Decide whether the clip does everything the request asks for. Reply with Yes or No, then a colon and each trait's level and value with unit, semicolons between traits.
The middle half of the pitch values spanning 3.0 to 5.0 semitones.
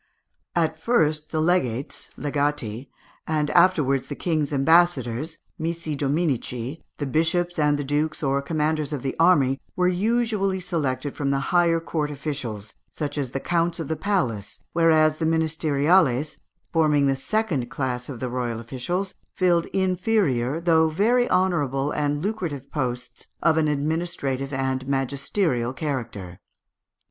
Yes: average, 4.0 semitones